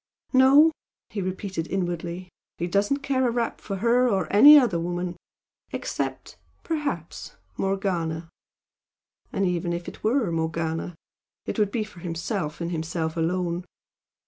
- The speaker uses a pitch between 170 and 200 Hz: Yes, medium, 185 Hz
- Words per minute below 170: Yes, slow, 135 wpm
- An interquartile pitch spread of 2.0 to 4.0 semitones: No, average, 4.7 semitones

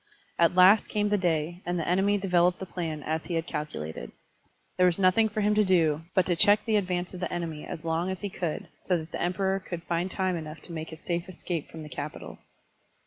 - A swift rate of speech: Yes, fast, 235 wpm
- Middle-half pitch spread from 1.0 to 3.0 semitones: Yes, narrow, 2.6 semitones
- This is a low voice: No, medium, 175 Hz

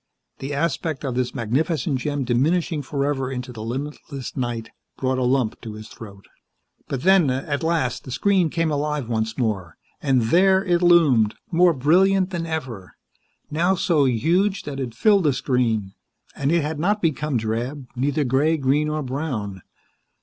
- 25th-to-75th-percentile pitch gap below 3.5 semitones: No, average, 4.7 semitones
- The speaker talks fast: No, average, 165 wpm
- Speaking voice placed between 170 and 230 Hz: No, medium, 140 Hz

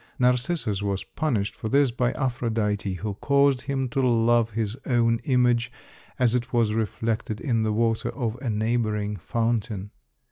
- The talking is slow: No, average, 150 wpm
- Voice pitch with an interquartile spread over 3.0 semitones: No, narrow, 2.6 semitones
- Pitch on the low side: Yes, low, 115 Hz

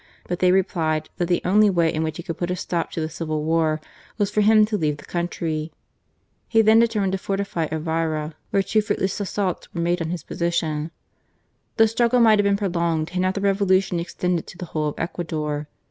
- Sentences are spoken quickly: Yes, fast, 215 wpm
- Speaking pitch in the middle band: Yes, medium, 175 Hz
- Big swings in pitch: No, average, 3.7 semitones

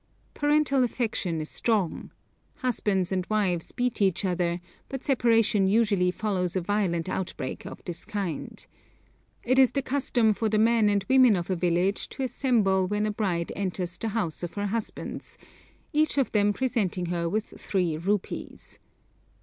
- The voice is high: Yes, high, 205 Hz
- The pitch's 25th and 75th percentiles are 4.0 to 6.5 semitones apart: Yes, average, 4.3 semitones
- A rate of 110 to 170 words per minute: Yes, average, 160 wpm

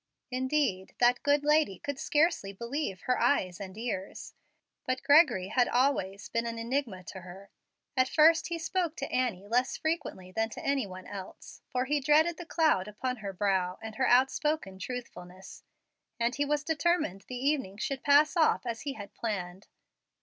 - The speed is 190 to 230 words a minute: No, average, 170 wpm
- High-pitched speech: Yes, very high, 250 Hz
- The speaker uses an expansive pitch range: Yes, wide, 6.8 semitones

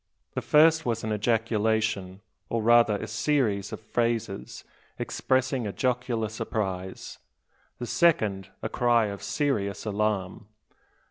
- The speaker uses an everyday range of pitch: Yes, average, 3.0 semitones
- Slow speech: Yes, slow, 120 wpm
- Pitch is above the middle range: No, low, 110 Hz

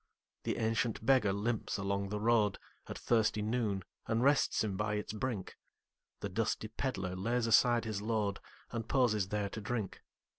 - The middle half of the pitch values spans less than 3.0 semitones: Yes, narrow, 2.5 semitones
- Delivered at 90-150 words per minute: Yes, average, 145 wpm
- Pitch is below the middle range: Yes, low, 110 Hz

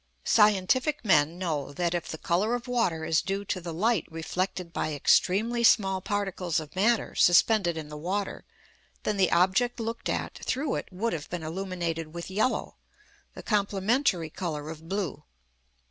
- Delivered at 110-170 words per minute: Yes, average, 160 wpm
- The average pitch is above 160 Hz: Yes, medium, 185 Hz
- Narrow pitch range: No, average, 4.4 semitones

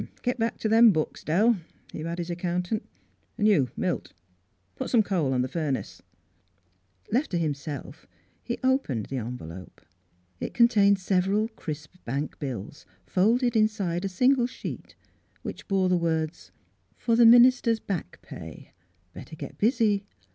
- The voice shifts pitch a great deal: Yes, wide, 6.7 semitones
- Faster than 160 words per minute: No, average, 150 wpm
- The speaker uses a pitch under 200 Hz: Yes, medium, 185 Hz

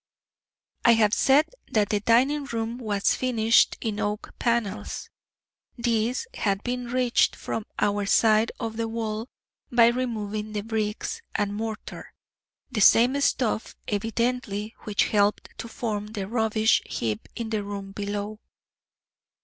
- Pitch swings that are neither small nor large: No, narrow, 2.2 semitones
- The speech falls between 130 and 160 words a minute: Yes, slow, 135 wpm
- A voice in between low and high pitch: No, high, 220 Hz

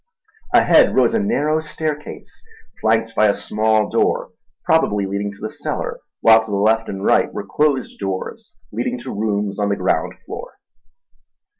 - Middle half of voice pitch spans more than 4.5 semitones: No, average, 4.2 semitones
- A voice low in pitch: Yes, low, 110 Hz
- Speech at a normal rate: Yes, average, 160 wpm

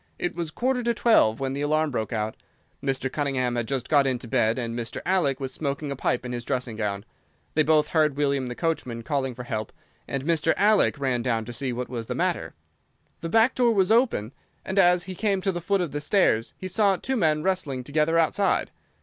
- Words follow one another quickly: Yes, fast, 220 wpm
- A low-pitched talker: No, medium, 145 Hz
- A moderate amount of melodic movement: No, wide, 6.2 semitones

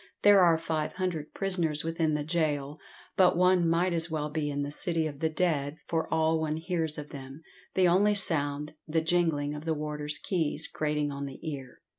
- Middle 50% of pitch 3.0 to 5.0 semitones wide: No, narrow, 2.4 semitones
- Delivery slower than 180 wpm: No, average, 195 wpm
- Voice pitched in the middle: Yes, medium, 160 Hz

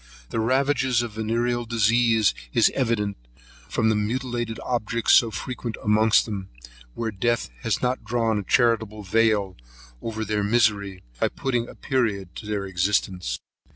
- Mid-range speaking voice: No, low, 110 Hz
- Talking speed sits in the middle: Yes, average, 150 wpm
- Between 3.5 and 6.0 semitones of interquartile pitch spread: No, narrow, 2.4 semitones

